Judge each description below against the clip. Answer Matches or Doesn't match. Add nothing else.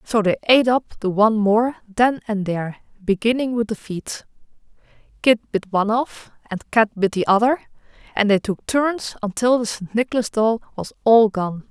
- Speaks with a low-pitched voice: Doesn't match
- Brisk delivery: Doesn't match